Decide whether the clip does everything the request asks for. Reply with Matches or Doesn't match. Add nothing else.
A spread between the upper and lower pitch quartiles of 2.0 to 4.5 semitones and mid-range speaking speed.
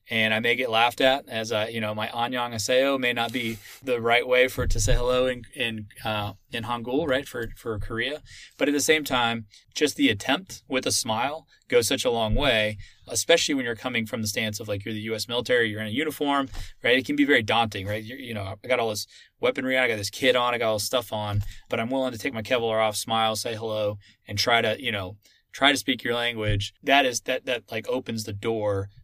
Doesn't match